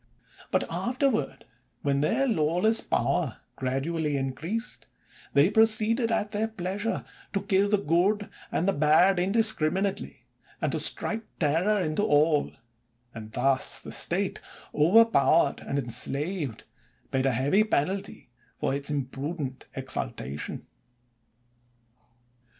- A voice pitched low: No, medium, 170 Hz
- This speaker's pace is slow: Yes, slow, 115 wpm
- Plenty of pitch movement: Yes, wide, 6.7 semitones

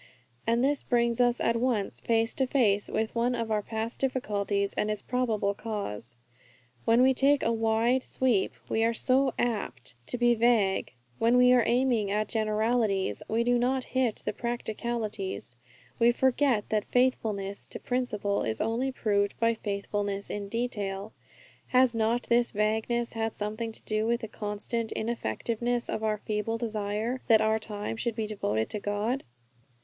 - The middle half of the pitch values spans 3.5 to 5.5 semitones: No, narrow, 2.6 semitones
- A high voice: Yes, high, 225 Hz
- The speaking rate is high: No, average, 165 wpm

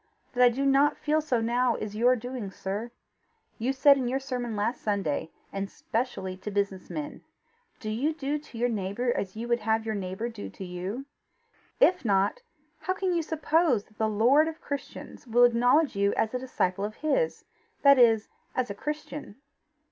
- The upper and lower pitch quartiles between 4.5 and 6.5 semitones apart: Yes, average, 5.0 semitones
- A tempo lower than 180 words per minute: No, average, 185 wpm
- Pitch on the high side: Yes, high, 240 Hz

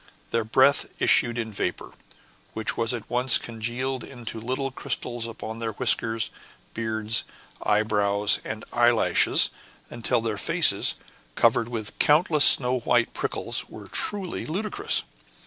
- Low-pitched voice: Yes, low, 115 Hz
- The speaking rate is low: Yes, slow, 125 wpm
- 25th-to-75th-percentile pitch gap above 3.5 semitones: No, narrow, 2.4 semitones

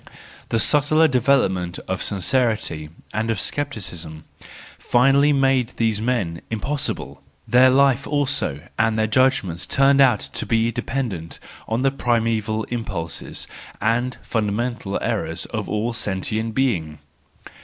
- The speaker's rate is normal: No, slow, 120 wpm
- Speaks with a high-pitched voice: No, low, 115 Hz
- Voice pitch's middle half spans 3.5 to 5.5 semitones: Yes, average, 4.6 semitones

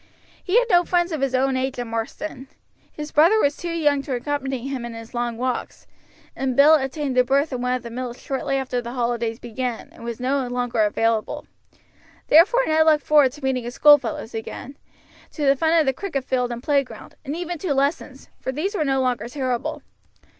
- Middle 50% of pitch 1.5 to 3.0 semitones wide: No, average, 3.4 semitones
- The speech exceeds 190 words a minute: Yes, fast, 205 wpm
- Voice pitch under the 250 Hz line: No, very high, 265 Hz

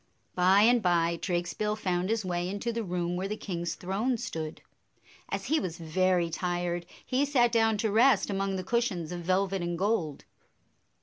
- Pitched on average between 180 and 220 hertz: Yes, medium, 185 Hz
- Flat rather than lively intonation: No, average, 3.9 semitones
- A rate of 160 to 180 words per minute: Yes, average, 175 wpm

